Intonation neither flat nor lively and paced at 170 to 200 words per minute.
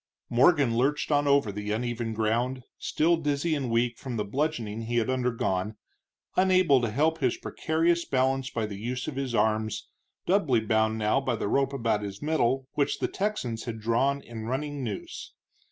Yes: average, 4.1 semitones; average, 175 wpm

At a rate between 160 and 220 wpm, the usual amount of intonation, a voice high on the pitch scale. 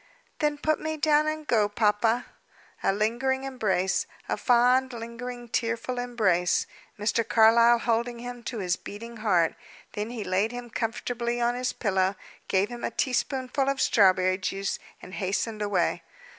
No: average, 150 wpm; average, 3.1 semitones; high, 235 Hz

